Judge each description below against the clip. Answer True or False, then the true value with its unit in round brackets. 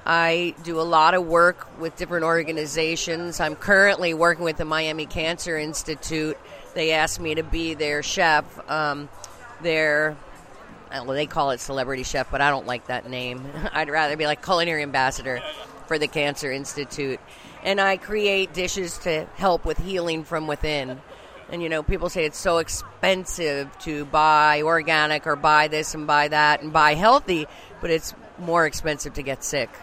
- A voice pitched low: False (155 Hz)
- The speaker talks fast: False (170 wpm)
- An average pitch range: False (2.3 semitones)